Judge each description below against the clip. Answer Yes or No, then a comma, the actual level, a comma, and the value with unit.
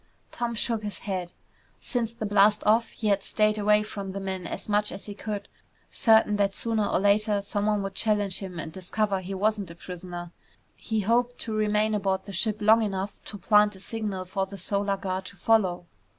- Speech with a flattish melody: Yes, narrow, 1.9 semitones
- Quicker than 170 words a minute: Yes, average, 200 wpm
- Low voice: No, high, 205 Hz